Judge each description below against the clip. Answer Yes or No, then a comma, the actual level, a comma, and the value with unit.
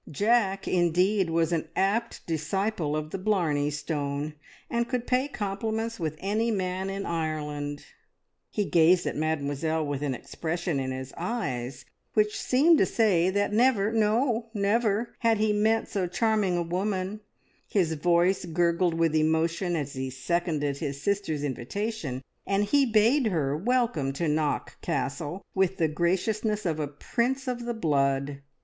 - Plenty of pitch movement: Yes, wide, 5.7 semitones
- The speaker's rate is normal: Yes, average, 150 wpm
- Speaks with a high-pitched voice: No, medium, 180 Hz